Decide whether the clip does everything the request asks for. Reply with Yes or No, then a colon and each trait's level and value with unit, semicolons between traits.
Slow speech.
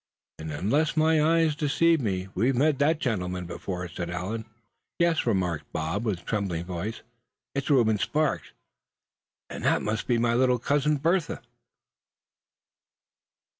Yes: slow, 130 wpm